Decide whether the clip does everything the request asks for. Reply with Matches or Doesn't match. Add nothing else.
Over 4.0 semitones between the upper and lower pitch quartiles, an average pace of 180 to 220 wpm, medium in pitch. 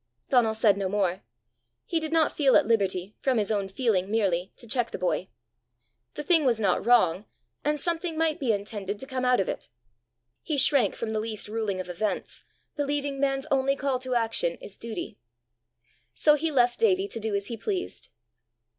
Doesn't match